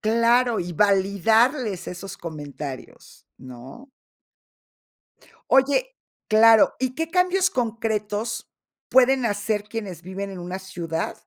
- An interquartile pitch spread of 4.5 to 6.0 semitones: Yes, average, 5.1 semitones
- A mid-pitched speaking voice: No, high, 215 Hz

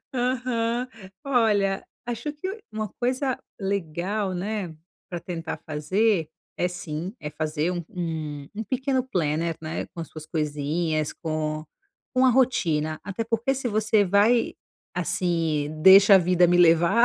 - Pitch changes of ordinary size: No, wide, 6.1 semitones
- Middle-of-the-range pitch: Yes, medium, 180 Hz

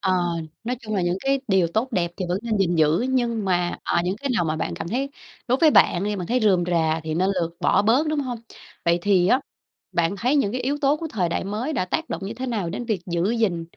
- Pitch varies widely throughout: Yes, wide, 6.1 semitones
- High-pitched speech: Yes, high, 200 Hz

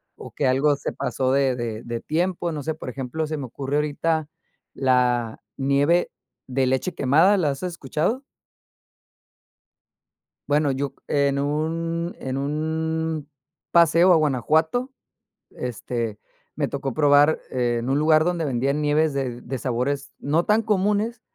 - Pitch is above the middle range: No, medium, 145 Hz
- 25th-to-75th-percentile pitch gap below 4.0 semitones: Yes, average, 3.4 semitones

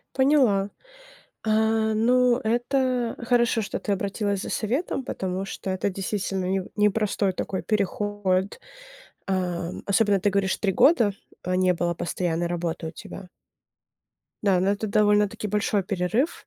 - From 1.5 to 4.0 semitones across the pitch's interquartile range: Yes, average, 2.8 semitones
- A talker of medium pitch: No, high, 200 Hz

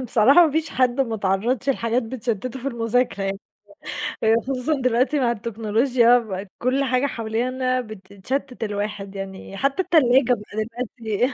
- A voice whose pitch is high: Yes, high, 240 Hz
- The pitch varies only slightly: No, average, 3.2 semitones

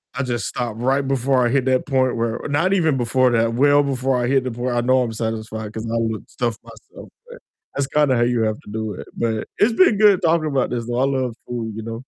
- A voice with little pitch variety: No, average, 3.1 semitones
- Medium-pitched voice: No, low, 125 Hz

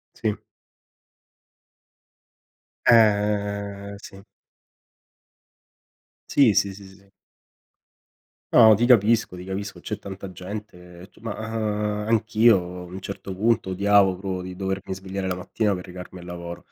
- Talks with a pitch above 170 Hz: No, low, 100 Hz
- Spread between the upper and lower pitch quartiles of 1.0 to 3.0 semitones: Yes, narrow, 2.4 semitones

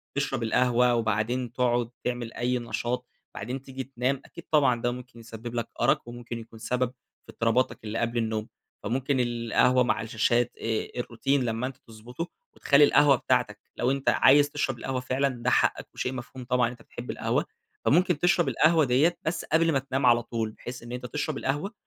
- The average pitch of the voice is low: Yes, low, 125 Hz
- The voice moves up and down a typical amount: No, narrow, 2.3 semitones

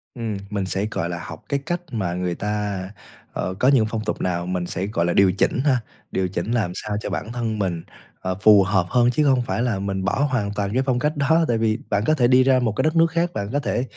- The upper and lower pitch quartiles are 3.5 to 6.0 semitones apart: Yes, average, 5.0 semitones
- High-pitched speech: No, low, 110 Hz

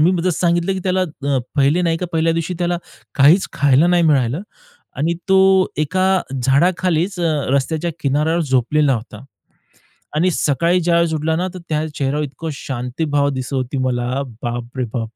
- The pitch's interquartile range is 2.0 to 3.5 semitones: No, average, 4.2 semitones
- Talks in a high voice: No, medium, 155 Hz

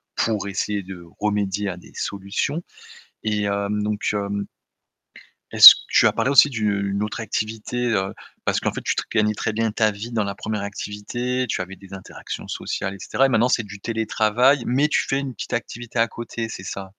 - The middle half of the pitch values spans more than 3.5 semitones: No, average, 2.8 semitones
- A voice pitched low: Yes, low, 105 Hz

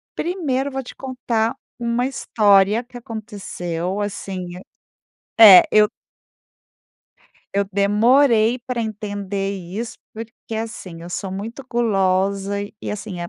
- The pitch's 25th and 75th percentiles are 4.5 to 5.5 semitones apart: No, average, 3.3 semitones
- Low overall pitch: No, high, 210 Hz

